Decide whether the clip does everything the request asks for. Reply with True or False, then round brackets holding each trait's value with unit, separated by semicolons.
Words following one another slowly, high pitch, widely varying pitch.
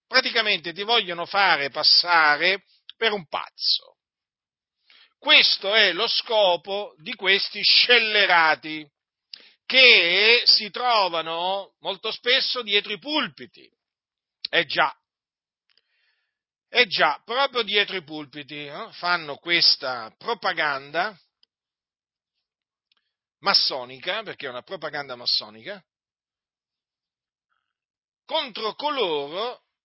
True (90 wpm; 200 Hz; 6.9 semitones)